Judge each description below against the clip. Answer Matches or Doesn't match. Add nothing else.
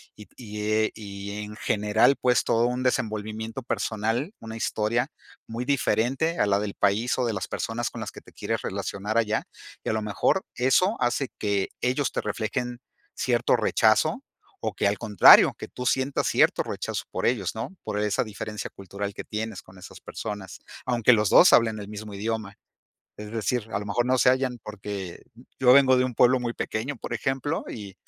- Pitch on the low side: Matches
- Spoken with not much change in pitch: Doesn't match